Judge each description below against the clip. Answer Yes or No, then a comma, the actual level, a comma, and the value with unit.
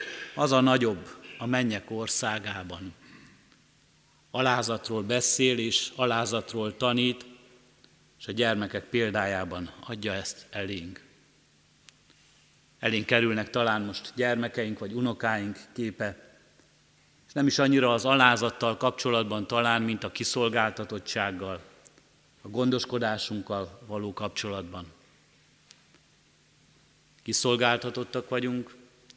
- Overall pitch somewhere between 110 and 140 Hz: Yes, low, 115 Hz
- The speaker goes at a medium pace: No, slow, 90 wpm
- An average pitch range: Yes, average, 3.1 semitones